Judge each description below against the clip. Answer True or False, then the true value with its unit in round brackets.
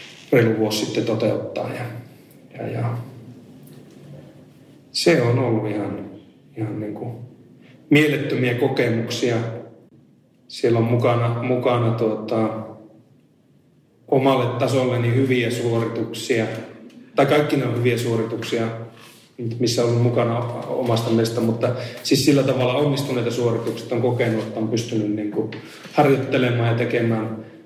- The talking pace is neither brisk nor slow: True (115 wpm)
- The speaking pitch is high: False (120 Hz)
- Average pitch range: False (1.8 semitones)